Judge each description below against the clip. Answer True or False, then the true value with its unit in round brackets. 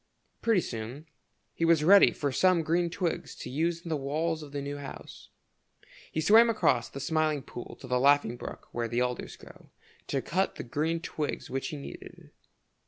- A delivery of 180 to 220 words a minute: True (185 wpm)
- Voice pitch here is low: False (150 Hz)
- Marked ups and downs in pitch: False (3.6 semitones)